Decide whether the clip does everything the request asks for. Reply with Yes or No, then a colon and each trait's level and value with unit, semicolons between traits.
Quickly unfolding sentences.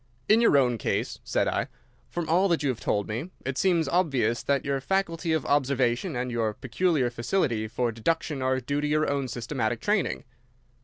No: average, 190 wpm